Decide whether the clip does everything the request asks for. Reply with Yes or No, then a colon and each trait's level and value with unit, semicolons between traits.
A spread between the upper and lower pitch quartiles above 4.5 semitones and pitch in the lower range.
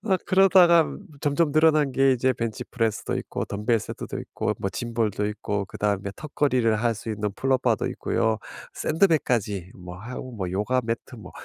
Yes: wide, 5.4 semitones; low, 120 Hz